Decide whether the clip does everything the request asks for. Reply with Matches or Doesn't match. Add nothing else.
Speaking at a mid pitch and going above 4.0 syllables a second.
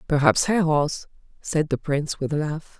Matches